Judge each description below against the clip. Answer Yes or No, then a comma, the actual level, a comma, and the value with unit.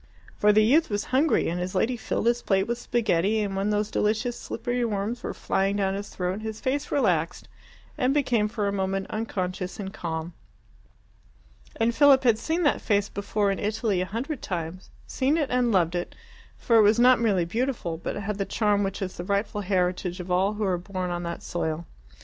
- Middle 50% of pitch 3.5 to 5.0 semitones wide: Yes, average, 4.0 semitones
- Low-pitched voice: No, high, 205 Hz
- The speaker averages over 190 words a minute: Yes, average, 200 wpm